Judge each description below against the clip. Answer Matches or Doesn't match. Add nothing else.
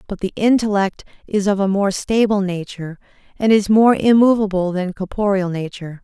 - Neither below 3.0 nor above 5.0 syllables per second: Doesn't match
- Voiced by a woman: Matches